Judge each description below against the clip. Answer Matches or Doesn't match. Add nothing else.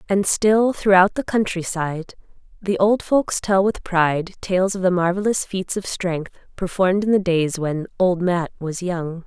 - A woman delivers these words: Matches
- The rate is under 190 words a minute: Matches